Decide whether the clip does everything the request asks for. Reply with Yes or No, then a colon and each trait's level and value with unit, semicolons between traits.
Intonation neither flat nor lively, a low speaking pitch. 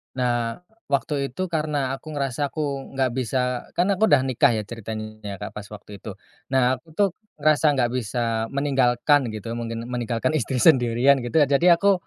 Yes: average, 3.6 semitones; low, 130 Hz